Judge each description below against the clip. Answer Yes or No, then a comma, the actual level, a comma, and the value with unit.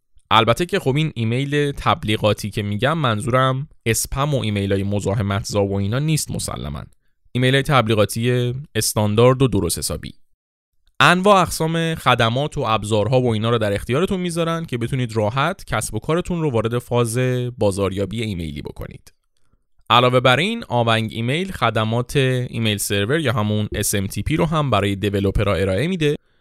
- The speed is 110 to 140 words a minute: No, average, 150 wpm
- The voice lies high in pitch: No, low, 120 Hz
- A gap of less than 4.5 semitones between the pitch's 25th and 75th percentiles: No, average, 5.0 semitones